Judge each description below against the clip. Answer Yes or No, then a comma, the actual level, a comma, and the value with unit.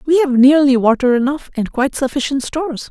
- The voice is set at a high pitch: Yes, very high, 270 Hz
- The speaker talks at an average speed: Yes, average, 185 wpm